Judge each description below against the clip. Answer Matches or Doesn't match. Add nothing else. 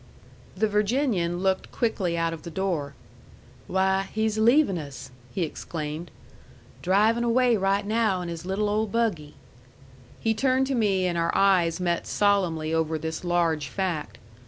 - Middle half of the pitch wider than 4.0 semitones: Matches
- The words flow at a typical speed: Matches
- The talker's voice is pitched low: Doesn't match